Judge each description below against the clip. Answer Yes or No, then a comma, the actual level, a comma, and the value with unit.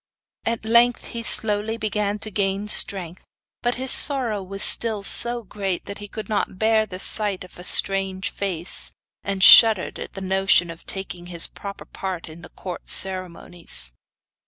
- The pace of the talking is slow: No, average, 165 wpm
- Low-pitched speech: No, high, 195 Hz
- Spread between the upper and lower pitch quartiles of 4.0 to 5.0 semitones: No, average, 2.8 semitones